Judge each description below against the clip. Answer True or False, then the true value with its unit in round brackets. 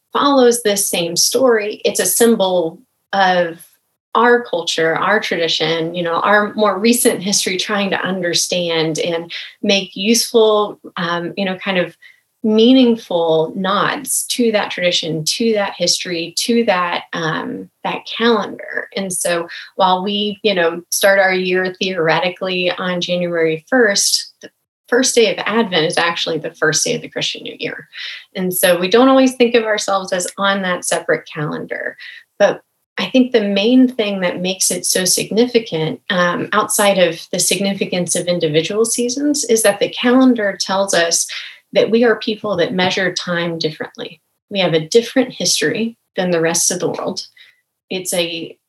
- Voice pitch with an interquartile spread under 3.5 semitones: False (4.6 semitones)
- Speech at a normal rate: True (160 wpm)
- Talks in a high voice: True (195 Hz)